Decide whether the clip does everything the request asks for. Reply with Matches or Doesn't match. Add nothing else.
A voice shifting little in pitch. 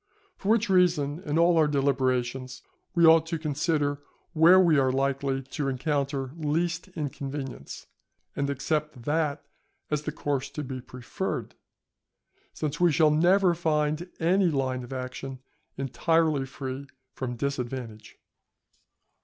Doesn't match